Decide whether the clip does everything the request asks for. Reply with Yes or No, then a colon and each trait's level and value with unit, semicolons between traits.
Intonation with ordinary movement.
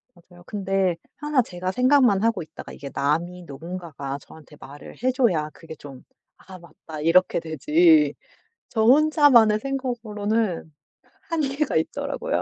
No: wide, 7.9 semitones